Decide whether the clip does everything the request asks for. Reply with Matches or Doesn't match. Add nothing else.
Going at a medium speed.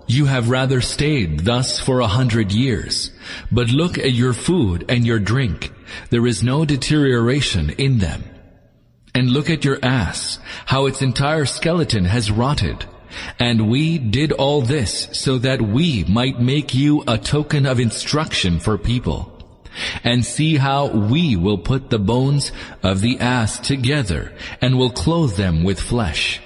Matches